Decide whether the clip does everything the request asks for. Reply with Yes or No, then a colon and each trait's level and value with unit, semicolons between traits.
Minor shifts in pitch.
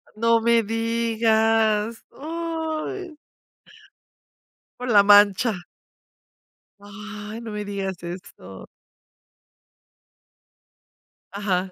Yes: narrow, 2.3 semitones